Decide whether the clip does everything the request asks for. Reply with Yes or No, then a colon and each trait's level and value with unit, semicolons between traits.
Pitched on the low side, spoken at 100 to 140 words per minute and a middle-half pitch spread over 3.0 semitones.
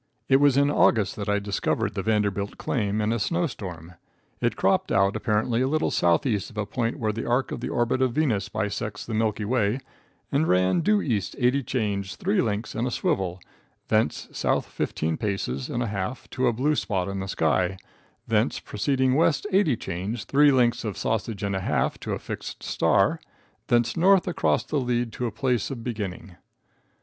No: low, 110 Hz; average, 190 wpm; average, 4.4 semitones